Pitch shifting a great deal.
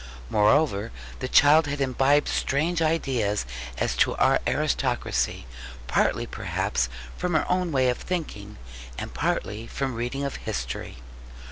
Yes: wide, 6.4 semitones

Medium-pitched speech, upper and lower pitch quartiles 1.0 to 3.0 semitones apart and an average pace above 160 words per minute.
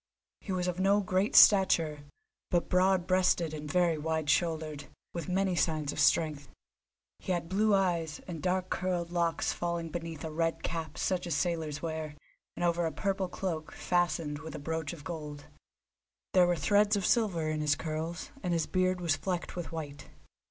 Yes: medium, 170 Hz; average, 2.7 semitones; average, 180 wpm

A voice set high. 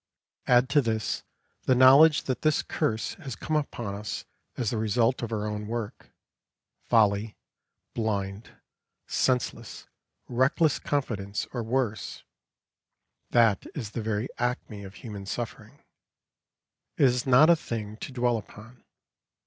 No: low, 115 Hz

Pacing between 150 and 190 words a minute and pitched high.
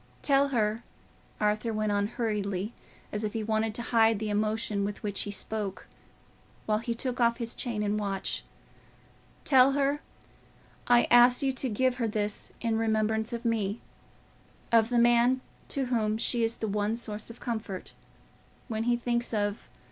Yes: average, 165 wpm; high, 225 Hz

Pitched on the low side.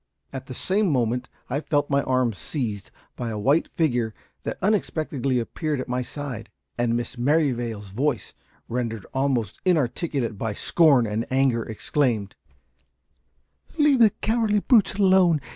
Yes: low, 130 Hz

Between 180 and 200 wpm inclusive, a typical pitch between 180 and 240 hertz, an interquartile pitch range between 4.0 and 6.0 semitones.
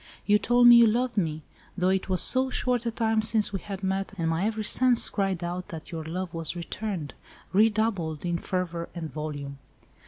Yes: average, 185 wpm; high, 190 Hz; average, 4.7 semitones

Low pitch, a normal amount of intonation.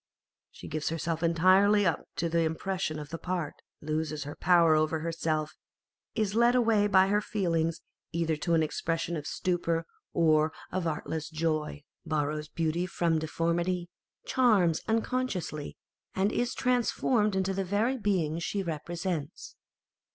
No: medium, 170 Hz; average, 3.5 semitones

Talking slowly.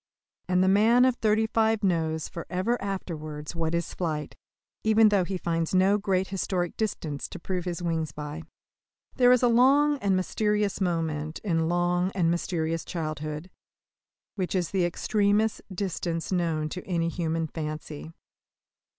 No: average, 150 wpm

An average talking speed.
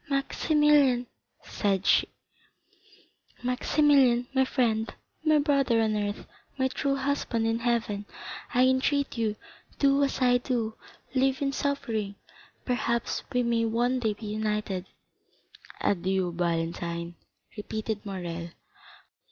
No: slow, 110 wpm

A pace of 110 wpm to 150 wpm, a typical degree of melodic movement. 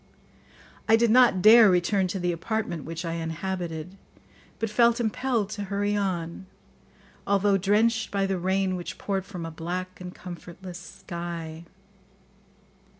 Yes: average, 140 wpm; average, 3.1 semitones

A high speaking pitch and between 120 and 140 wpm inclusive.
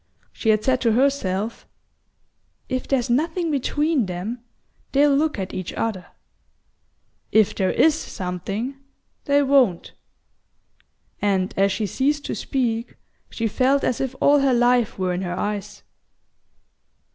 Yes: high, 240 Hz; slow, 135 wpm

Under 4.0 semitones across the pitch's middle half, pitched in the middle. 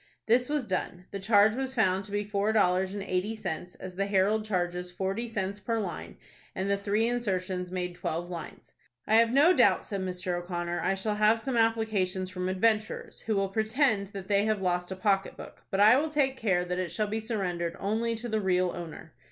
No: average, 3.2 semitones; high, 200 Hz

